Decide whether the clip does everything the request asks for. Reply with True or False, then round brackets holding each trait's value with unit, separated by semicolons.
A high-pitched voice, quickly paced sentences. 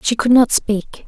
True (230 Hz; 225 wpm)